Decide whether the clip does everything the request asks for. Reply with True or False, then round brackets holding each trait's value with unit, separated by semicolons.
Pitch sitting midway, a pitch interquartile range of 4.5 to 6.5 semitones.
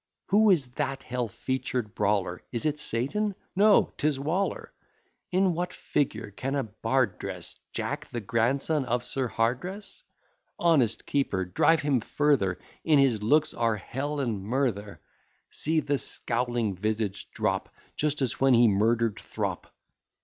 False (125 Hz; 5.1 semitones)